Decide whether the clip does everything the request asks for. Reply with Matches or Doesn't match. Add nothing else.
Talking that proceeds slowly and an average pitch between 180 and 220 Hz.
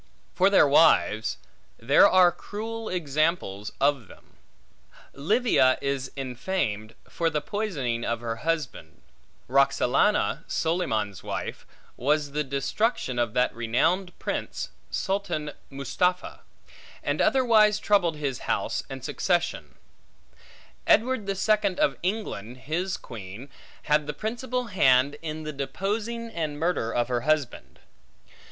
Doesn't match